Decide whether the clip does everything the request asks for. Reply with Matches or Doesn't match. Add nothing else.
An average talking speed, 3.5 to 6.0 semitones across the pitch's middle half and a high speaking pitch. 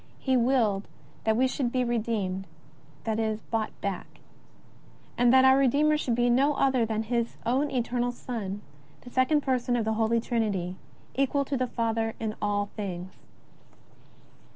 Doesn't match